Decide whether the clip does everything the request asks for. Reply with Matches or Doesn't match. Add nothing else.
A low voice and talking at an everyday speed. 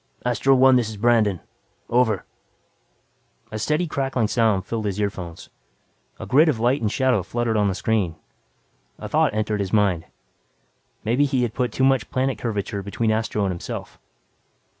Matches